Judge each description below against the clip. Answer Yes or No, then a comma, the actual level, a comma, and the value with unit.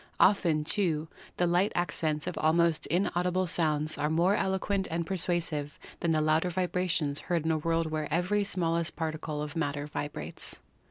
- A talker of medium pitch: Yes, medium, 165 Hz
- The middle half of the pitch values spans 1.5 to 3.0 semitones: Yes, narrow, 2.6 semitones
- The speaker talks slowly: No, average, 160 wpm